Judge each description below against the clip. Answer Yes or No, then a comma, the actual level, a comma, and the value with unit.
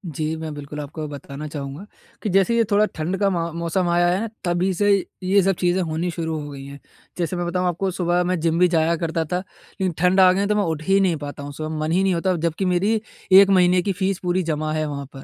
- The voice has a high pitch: No, medium, 175 Hz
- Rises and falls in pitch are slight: No, average, 3.2 semitones